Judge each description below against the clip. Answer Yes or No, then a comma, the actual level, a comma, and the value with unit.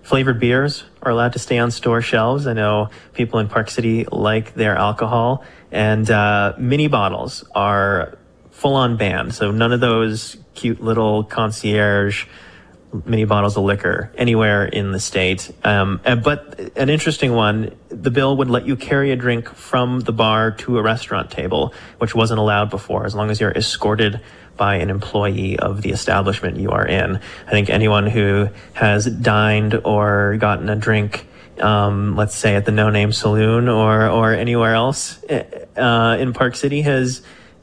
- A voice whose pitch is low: Yes, low, 110 Hz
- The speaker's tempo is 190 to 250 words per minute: No, average, 170 wpm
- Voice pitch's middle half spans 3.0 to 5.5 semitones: No, narrow, 2.6 semitones